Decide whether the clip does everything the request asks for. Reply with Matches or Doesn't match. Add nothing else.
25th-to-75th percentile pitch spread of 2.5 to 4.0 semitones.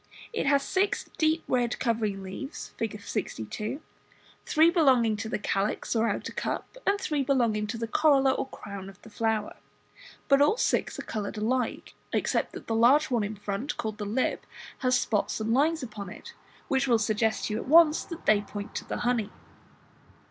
Doesn't match